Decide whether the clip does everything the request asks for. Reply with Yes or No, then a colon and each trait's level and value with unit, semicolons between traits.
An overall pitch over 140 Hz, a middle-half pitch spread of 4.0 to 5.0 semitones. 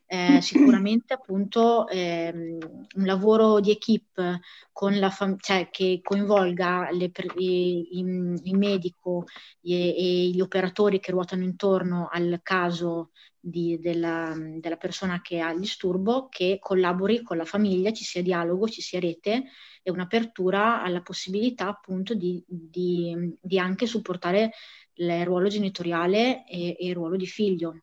No: medium, 185 Hz; narrow, 2.4 semitones